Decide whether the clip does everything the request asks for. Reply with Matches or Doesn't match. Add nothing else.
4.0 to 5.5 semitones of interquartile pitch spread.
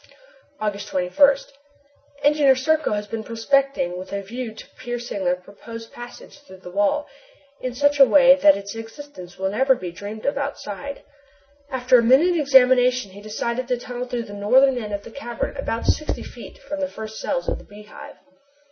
Matches